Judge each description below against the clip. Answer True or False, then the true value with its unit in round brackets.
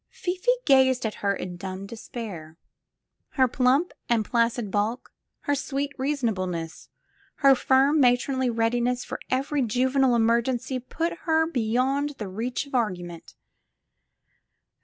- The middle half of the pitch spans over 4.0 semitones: False (3.7 semitones)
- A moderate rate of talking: False (120 wpm)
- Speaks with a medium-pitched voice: False (245 Hz)